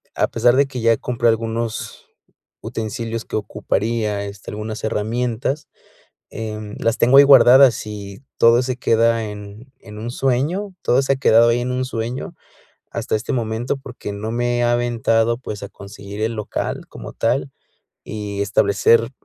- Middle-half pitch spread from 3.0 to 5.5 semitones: No, narrow, 2.4 semitones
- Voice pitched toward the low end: Yes, low, 115 Hz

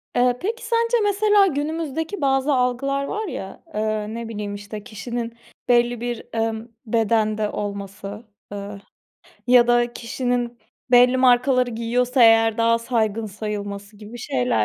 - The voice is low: No, high, 235 Hz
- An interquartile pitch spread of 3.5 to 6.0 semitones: No, average, 3.1 semitones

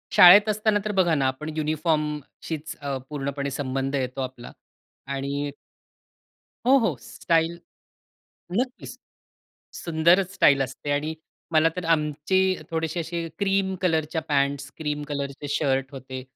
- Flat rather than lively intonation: No, average, 3.5 semitones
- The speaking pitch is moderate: Yes, medium, 150 Hz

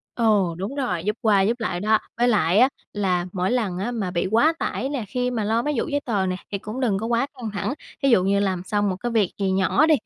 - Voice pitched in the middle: No, high, 215 Hz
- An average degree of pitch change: Yes, average, 4.2 semitones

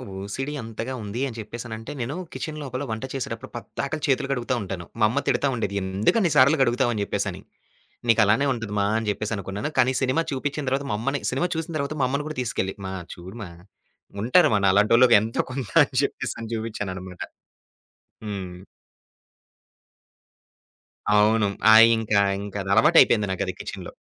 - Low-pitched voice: Yes, low, 115 Hz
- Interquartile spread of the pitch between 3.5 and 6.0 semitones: Yes, average, 4.7 semitones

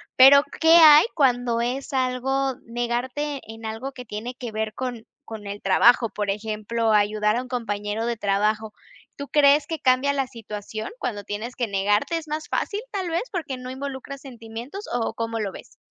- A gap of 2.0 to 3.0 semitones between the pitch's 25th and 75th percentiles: No, average, 3.9 semitones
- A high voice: Yes, high, 240 Hz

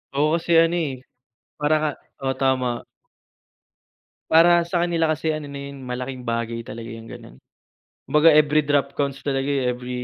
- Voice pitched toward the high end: No, medium, 140 Hz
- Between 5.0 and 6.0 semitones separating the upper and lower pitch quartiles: No, average, 3.7 semitones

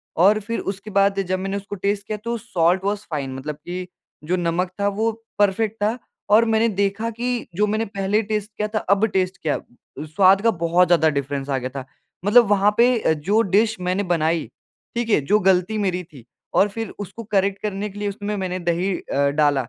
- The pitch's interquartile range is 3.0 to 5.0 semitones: Yes, average, 3.3 semitones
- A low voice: No, high, 195 Hz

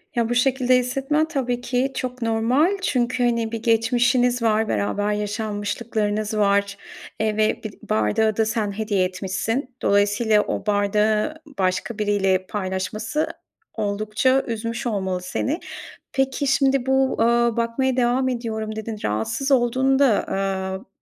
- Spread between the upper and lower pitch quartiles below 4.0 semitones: Yes, average, 3.5 semitones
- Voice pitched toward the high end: Yes, high, 225 Hz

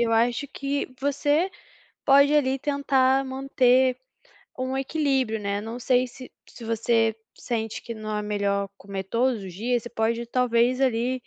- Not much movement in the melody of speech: No, average, 3.0 semitones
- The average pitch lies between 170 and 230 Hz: No, high, 245 Hz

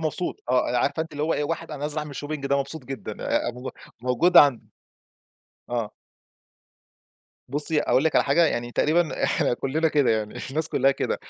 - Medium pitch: Yes, medium, 145 Hz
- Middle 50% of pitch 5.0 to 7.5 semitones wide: No, average, 3.6 semitones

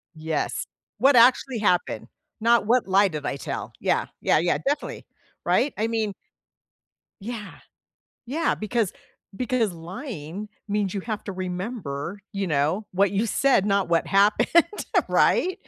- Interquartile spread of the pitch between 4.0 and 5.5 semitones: Yes, average, 4.4 semitones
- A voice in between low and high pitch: No, high, 205 Hz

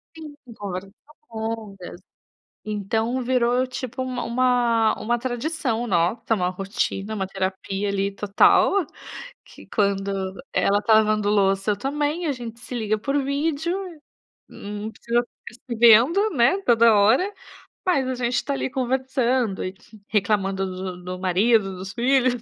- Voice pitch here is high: Yes, high, 225 Hz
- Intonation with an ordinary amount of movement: Yes, average, 4.5 semitones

